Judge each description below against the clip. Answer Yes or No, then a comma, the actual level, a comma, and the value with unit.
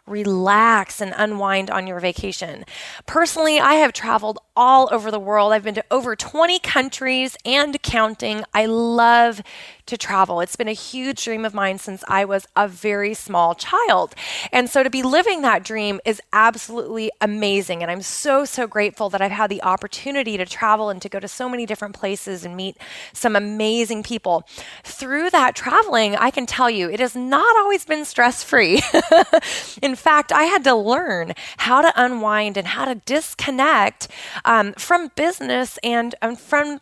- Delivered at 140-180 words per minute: Yes, average, 175 wpm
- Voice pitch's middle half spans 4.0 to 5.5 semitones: Yes, average, 4.5 semitones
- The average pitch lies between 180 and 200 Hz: No, high, 225 Hz